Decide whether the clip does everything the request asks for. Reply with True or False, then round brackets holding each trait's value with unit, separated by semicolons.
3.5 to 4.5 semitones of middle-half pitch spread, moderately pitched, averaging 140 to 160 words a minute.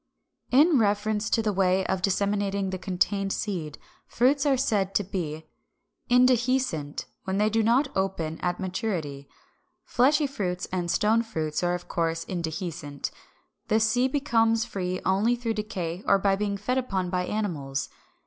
False (4.0 semitones; 200 Hz; 150 wpm)